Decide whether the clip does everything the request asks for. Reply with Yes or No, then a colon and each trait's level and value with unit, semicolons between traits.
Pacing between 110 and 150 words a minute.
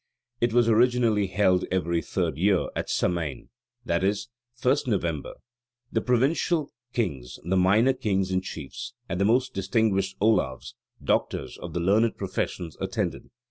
Yes: average, 140 wpm